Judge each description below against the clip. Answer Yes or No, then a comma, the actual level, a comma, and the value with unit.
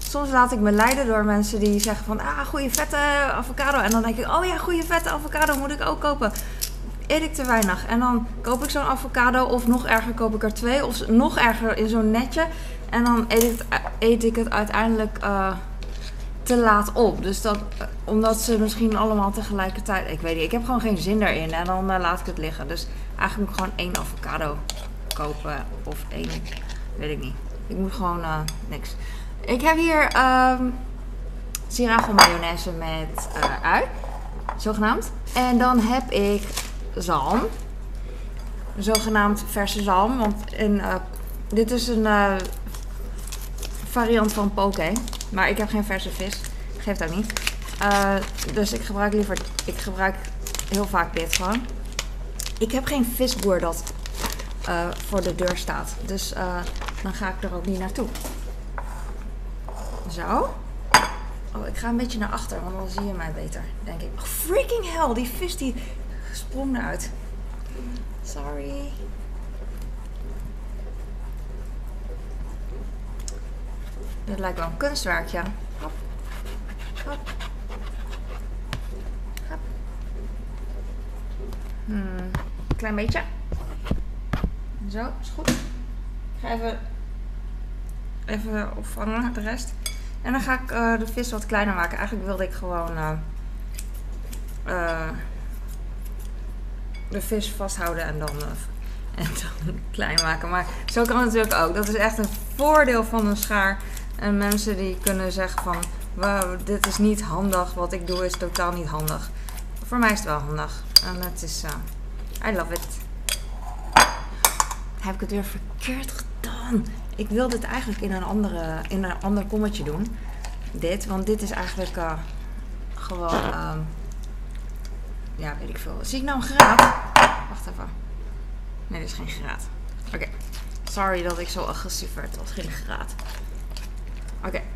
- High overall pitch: Yes, high, 205 Hz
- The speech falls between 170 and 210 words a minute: No, average, 150 wpm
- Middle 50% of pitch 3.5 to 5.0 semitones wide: Yes, average, 4.7 semitones